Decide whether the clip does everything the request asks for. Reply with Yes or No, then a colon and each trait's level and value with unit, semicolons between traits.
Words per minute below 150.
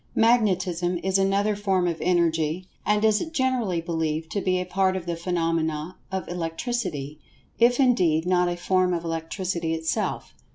No: average, 155 wpm